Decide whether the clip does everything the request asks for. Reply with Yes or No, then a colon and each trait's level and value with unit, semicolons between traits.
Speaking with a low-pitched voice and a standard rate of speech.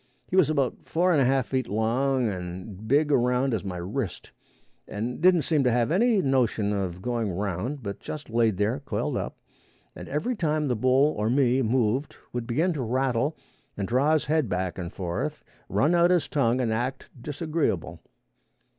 Yes: low, 125 Hz; average, 180 wpm